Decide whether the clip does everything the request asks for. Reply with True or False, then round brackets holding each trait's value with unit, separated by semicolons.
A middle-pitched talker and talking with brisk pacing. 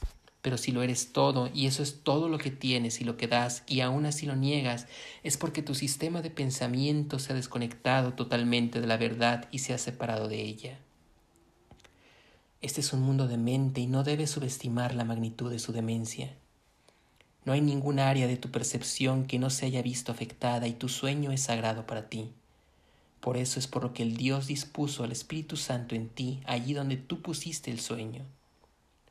False (125 Hz; 195 wpm)